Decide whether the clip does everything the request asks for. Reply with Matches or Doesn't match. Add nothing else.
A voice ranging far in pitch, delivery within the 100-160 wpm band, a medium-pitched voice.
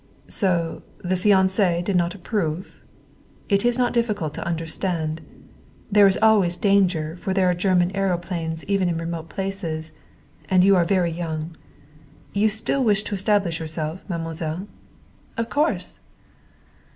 Doesn't match